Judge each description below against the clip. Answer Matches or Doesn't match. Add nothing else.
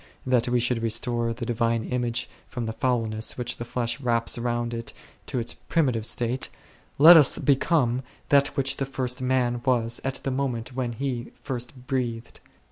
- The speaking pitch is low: Matches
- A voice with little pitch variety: Matches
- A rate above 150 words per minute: Matches